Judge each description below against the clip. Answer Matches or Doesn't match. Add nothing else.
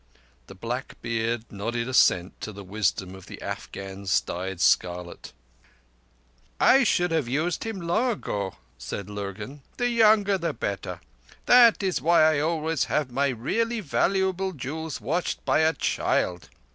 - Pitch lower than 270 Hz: Matches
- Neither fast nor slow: Matches